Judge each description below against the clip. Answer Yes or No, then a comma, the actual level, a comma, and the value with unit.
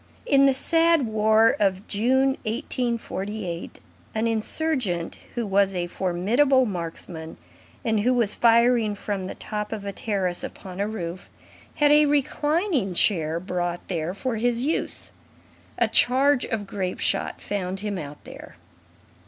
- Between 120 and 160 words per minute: Yes, average, 140 wpm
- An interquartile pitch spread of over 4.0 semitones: Yes, average, 5.1 semitones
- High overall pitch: Yes, high, 215 Hz